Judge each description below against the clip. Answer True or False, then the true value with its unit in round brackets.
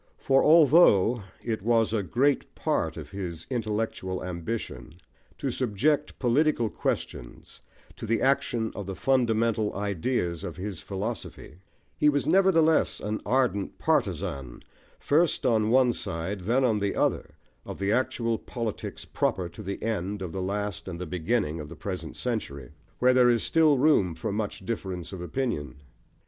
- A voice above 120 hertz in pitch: False (110 Hz)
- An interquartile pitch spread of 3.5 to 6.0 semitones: True (5.2 semitones)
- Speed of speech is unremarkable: True (155 wpm)